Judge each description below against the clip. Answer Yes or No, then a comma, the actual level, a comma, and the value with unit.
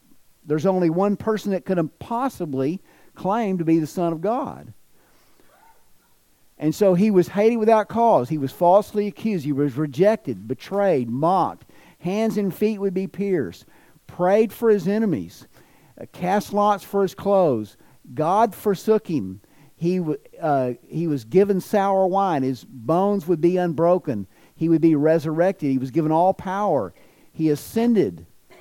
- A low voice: No, medium, 185 Hz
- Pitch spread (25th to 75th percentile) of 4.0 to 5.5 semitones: Yes, average, 4.5 semitones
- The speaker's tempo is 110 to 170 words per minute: Yes, average, 150 wpm